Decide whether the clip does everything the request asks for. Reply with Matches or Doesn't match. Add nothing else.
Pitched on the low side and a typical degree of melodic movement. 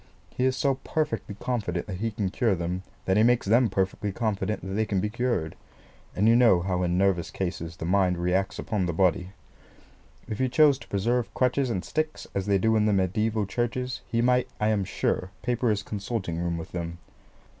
Matches